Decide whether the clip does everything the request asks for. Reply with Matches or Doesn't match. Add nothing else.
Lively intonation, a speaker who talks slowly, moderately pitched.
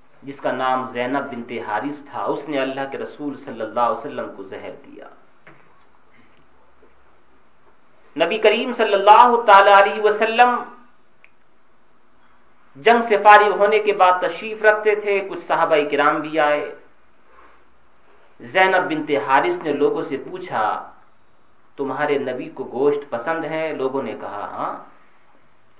Matches